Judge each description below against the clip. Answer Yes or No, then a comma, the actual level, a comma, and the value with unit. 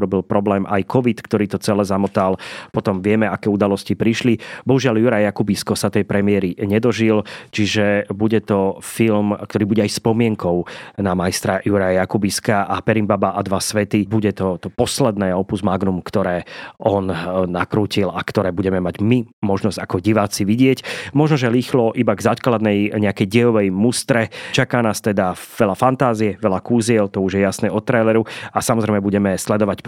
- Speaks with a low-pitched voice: Yes, low, 105 Hz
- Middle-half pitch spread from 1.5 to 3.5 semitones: Yes, narrow, 2.4 semitones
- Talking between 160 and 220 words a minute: Yes, fast, 165 wpm